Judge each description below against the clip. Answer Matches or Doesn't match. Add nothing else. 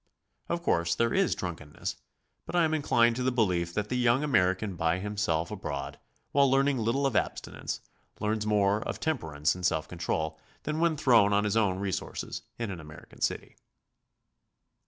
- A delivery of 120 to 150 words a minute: Doesn't match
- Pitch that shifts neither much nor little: Doesn't match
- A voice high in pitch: Doesn't match